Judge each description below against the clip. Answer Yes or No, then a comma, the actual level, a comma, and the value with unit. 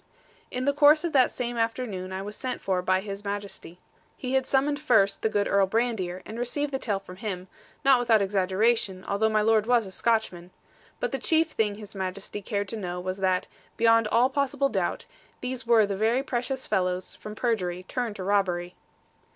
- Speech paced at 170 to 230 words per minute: Yes, average, 195 wpm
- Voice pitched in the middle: No, high, 215 Hz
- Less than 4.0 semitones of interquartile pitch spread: No, average, 4.4 semitones